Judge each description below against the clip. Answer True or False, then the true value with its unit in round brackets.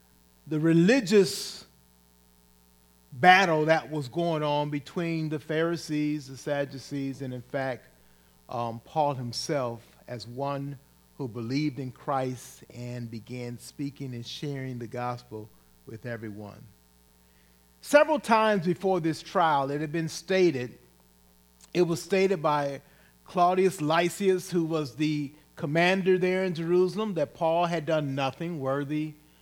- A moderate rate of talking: False (125 wpm)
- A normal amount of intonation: False (6.0 semitones)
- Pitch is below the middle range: False (145 Hz)